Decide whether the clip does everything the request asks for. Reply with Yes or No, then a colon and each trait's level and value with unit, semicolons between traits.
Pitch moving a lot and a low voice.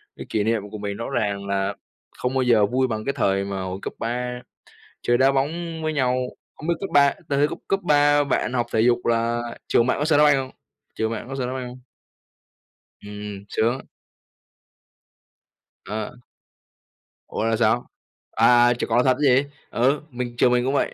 No: average, 3.7 semitones; low, 125 Hz